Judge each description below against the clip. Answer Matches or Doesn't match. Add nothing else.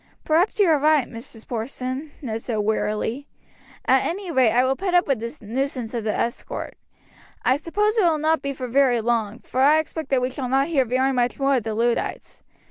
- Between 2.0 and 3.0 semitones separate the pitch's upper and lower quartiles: Doesn't match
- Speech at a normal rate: Doesn't match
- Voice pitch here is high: Matches